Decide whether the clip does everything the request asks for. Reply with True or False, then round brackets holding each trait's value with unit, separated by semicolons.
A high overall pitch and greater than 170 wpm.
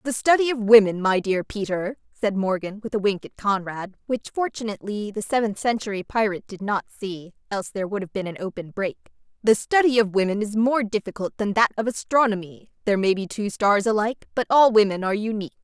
True (210 Hz; 200 wpm)